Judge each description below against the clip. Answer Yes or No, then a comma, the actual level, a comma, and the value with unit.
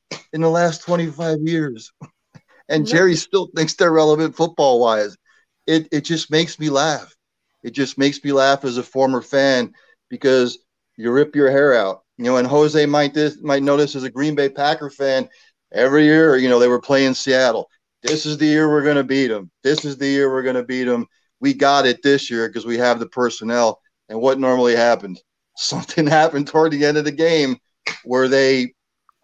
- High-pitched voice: No, medium, 140 Hz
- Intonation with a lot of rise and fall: No, average, 3.3 semitones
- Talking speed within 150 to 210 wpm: Yes, average, 200 wpm